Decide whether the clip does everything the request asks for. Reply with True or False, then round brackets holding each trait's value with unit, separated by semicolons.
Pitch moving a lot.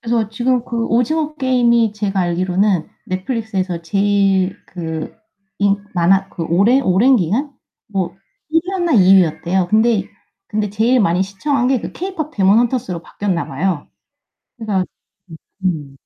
False (4.5 semitones)